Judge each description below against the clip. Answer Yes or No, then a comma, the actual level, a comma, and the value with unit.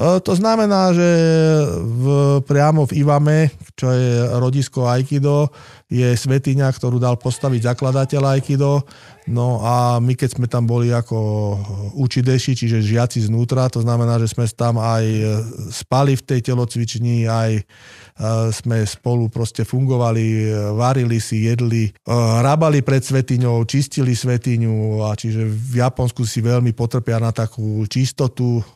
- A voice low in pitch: Yes, low, 120 Hz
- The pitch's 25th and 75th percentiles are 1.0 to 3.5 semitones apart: Yes, average, 2.7 semitones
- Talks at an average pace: Yes, average, 130 wpm